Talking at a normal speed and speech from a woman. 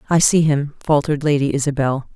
Yes: average, 165 wpm; female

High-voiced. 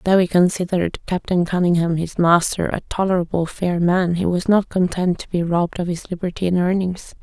No: medium, 175 Hz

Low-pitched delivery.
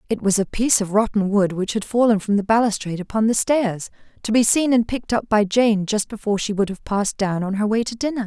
No: high, 215 Hz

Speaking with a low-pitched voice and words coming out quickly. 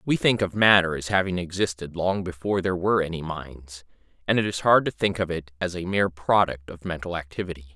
Yes: very low, 90 Hz; fast, 215 wpm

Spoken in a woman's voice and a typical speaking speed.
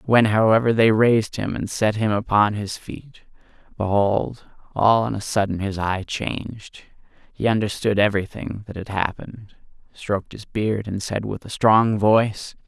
No: male; average, 160 wpm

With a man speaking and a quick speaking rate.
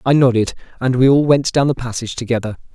Yes: male; fast, 220 wpm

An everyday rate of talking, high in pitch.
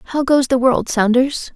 Yes: average, 195 wpm; very high, 260 Hz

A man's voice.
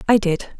No: female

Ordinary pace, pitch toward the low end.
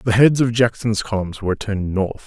No: fast, 210 wpm; low, 110 Hz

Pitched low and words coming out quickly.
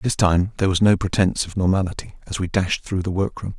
Yes: very low, 95 Hz; fast, 235 wpm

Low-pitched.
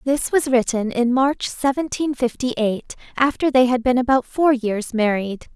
No: very high, 250 Hz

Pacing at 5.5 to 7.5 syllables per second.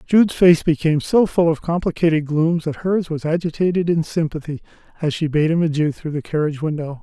Yes: 5.9 syllables/s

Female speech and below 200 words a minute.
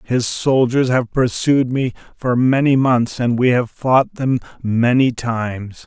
No: male; average, 155 wpm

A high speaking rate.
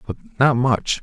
No: average, 175 wpm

